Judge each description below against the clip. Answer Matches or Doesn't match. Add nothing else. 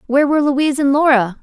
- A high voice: Matches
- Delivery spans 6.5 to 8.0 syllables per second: Matches